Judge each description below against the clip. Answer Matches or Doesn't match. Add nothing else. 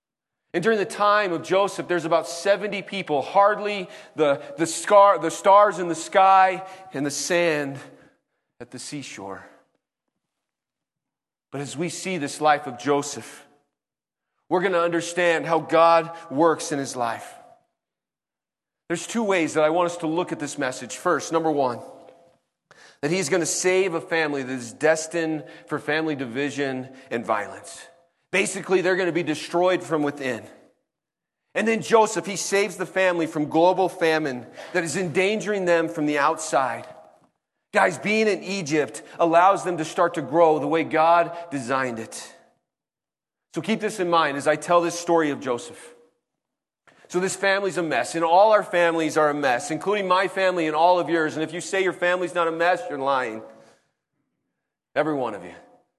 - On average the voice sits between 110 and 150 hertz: Doesn't match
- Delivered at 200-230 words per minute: Doesn't match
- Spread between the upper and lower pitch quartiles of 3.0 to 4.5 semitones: Matches